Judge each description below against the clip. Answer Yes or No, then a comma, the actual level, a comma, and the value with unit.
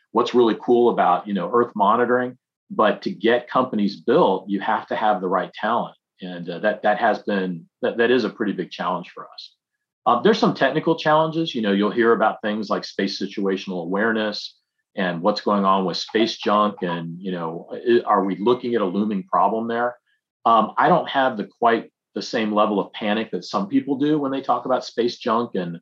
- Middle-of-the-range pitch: No, low, 105 Hz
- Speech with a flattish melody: No, average, 3.8 semitones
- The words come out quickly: Yes, fast, 210 wpm